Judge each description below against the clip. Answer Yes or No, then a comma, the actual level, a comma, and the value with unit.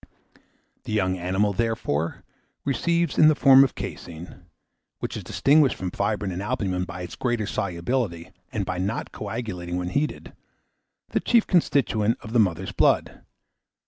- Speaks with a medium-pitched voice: No, low, 105 Hz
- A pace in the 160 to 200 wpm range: No, average, 145 wpm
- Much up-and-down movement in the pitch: Yes, wide, 5.9 semitones